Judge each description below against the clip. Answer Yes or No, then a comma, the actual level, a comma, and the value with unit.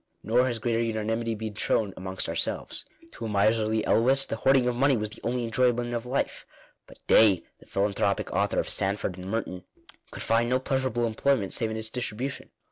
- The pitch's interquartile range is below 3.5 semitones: Yes, narrow, 2.5 semitones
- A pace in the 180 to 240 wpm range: Yes, average, 195 wpm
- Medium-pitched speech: No, low, 115 Hz